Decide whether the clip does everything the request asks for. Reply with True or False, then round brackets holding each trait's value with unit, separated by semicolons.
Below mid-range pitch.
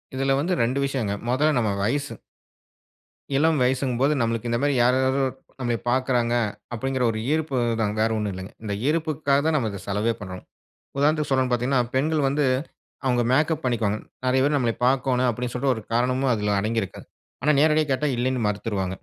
True (130 Hz)